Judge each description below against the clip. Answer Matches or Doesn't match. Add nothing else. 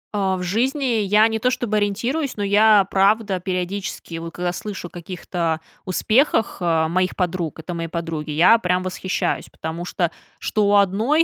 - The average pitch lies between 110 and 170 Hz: Doesn't match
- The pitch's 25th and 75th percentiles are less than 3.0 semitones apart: Doesn't match